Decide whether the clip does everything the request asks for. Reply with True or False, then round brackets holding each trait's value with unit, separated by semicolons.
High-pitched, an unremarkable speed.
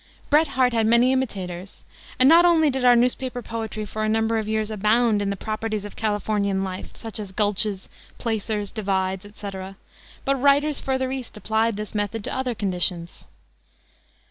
True (220 Hz; 170 wpm)